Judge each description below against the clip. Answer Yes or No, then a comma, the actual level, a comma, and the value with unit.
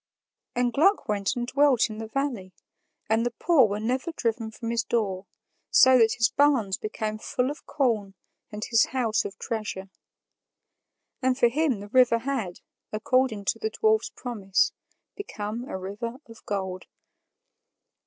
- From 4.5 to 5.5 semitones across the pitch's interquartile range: No, average, 3.7 semitones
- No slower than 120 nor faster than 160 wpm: Yes, average, 155 wpm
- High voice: Yes, high, 230 Hz